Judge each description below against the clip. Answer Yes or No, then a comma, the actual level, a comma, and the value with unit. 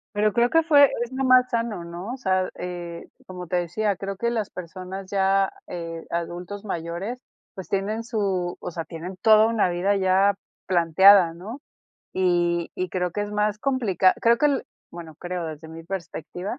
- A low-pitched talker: No, high, 190 Hz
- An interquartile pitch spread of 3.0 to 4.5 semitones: Yes, average, 3.6 semitones